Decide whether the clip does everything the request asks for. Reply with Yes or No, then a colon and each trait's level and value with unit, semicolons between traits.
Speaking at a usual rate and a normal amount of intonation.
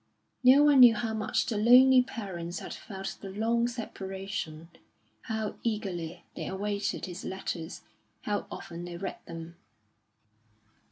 No: slow, 130 wpm; average, 4.7 semitones